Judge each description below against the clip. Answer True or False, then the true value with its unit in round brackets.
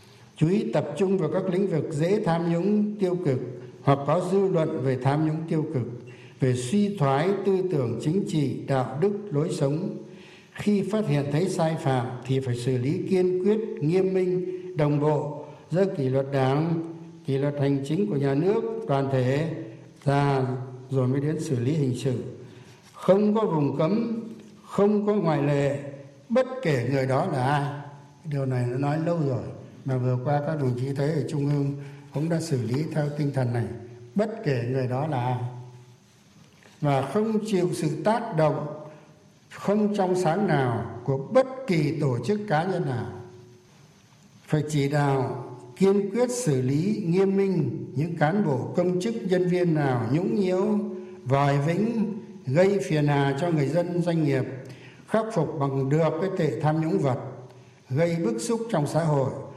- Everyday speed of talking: True (175 wpm)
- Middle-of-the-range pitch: True (150 Hz)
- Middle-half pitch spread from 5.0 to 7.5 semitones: True (5.3 semitones)